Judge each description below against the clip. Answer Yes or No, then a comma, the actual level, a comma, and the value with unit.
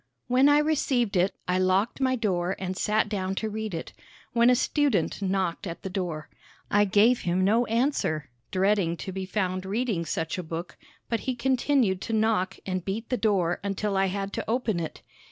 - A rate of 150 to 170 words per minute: No, average, 190 wpm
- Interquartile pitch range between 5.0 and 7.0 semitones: No, average, 3.8 semitones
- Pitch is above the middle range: Yes, high, 200 Hz